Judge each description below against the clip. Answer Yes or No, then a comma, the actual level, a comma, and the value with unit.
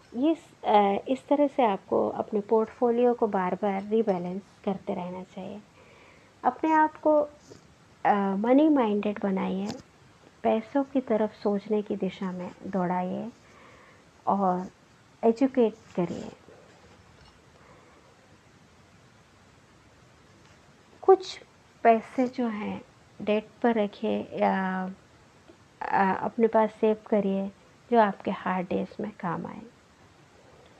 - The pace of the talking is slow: Yes, slow, 95 wpm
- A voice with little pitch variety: No, average, 3.7 semitones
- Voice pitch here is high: Yes, high, 215 Hz